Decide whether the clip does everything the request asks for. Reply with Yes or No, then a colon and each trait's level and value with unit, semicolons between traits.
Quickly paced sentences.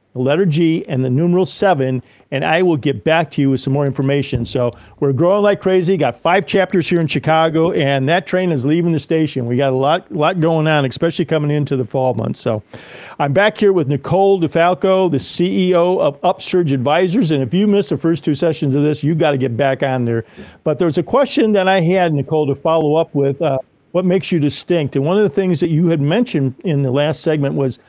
Yes: fast, 230 wpm